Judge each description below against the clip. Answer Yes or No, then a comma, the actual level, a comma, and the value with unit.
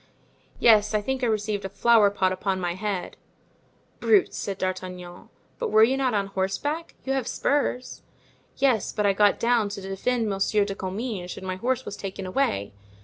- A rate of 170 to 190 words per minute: Yes, average, 180 wpm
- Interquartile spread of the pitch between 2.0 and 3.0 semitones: No, average, 4.1 semitones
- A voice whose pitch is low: No, high, 205 Hz